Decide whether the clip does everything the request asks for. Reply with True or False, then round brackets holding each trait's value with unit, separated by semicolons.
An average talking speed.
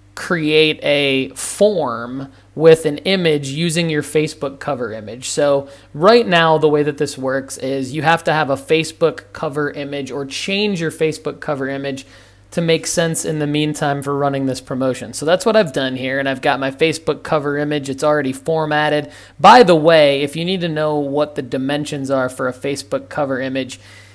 True (190 wpm)